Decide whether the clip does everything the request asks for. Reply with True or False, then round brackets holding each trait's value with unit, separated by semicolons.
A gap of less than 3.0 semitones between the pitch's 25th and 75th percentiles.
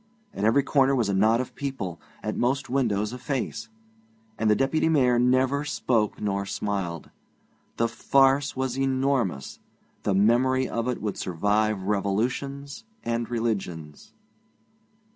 False (4.5 semitones)